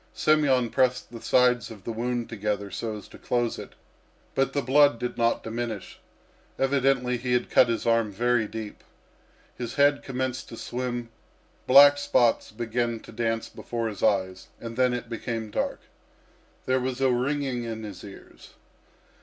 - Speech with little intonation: Yes, narrow, 2.2 semitones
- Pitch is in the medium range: No, low, 120 Hz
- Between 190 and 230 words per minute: No, average, 160 wpm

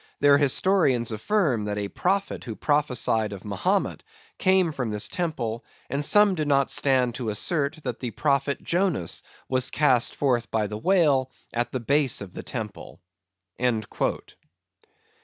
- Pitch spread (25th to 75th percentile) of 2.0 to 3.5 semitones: No, average, 5.2 semitones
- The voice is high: No, low, 130 Hz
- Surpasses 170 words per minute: No, average, 145 wpm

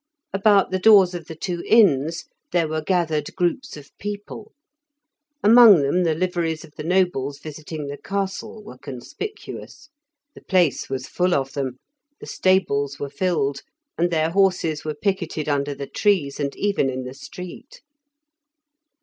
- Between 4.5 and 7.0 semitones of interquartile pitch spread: Yes, average, 5.0 semitones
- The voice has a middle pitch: Yes, medium, 165 Hz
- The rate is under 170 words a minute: Yes, average, 150 wpm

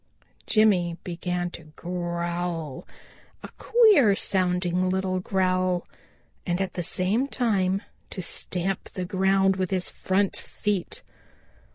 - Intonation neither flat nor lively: No, narrow, 1.6 semitones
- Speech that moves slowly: Yes, slow, 110 wpm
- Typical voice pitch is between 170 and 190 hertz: Yes, medium, 185 Hz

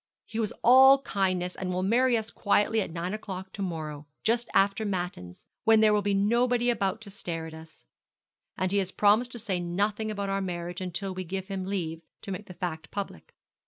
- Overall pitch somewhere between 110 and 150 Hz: No, high, 195 Hz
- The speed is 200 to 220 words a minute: Yes, fast, 205 wpm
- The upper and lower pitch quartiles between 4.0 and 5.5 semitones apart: No, average, 3.3 semitones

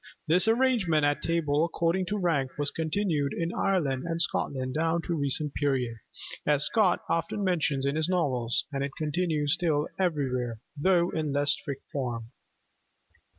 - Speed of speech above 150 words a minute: Yes, average, 160 wpm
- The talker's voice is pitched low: No, medium, 155 Hz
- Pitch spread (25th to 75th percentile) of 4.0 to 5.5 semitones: No, average, 3.5 semitones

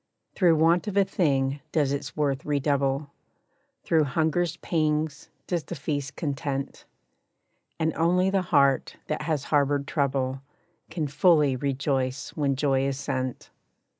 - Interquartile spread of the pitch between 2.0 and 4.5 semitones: Yes, average, 2.7 semitones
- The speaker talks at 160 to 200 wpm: No, slow, 135 wpm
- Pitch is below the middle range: No, medium, 145 Hz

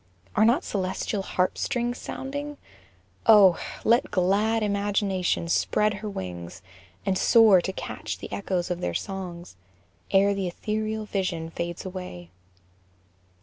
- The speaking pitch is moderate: No, high, 195 Hz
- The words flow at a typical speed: No, slow, 125 wpm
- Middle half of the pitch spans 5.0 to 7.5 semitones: No, average, 3.1 semitones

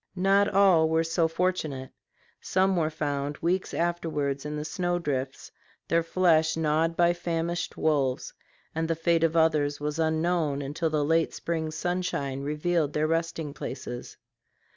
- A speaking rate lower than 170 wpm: Yes, average, 145 wpm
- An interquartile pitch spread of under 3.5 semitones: Yes, narrow, 2.4 semitones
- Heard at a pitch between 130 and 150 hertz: No, medium, 160 Hz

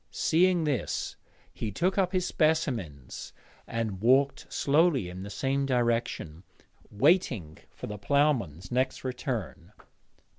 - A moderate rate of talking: No, slow, 115 wpm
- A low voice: Yes, low, 125 Hz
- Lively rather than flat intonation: Yes, wide, 7.0 semitones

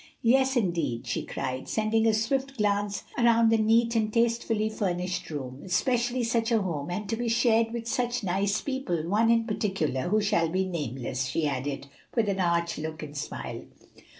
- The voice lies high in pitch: Yes, high, 210 Hz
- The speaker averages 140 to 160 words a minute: No, average, 180 wpm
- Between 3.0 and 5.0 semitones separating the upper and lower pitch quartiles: No, wide, 5.6 semitones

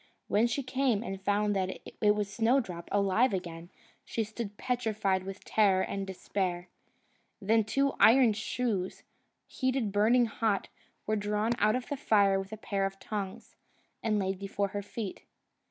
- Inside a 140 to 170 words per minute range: Yes, average, 155 wpm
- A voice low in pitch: No, high, 205 Hz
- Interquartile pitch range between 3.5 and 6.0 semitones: No, average, 2.7 semitones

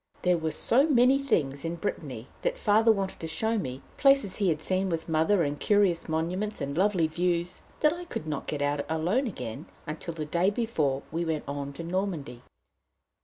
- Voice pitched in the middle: Yes, medium, 170 Hz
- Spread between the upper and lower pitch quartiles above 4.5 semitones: Yes, average, 5.0 semitones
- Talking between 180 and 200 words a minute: Yes, average, 190 wpm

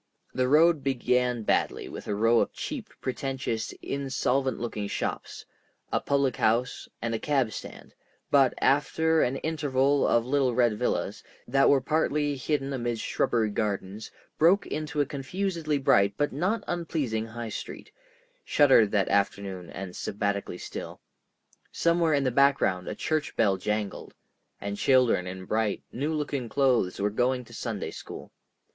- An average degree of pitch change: Yes, average, 4.8 semitones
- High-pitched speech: No, low, 130 Hz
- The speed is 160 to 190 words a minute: No, average, 150 wpm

